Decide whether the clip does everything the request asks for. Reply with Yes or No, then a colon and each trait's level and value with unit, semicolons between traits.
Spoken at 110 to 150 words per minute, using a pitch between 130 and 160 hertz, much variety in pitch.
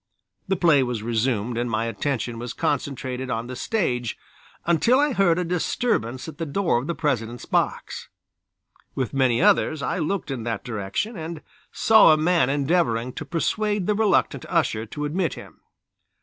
No: average, 165 wpm; medium, 140 Hz; wide, 6.5 semitones